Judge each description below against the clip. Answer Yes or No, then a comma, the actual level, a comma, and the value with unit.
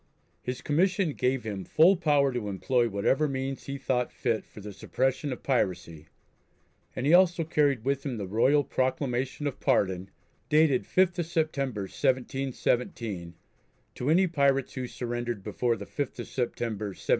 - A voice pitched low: Yes, low, 130 Hz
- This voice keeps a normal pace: Yes, average, 155 wpm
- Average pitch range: Yes, average, 4.0 semitones